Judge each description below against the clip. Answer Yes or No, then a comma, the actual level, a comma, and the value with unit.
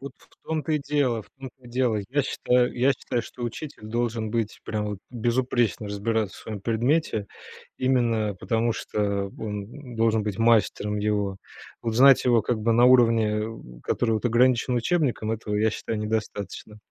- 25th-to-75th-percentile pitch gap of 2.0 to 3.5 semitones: Yes, narrow, 2.6 semitones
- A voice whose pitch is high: No, low, 115 Hz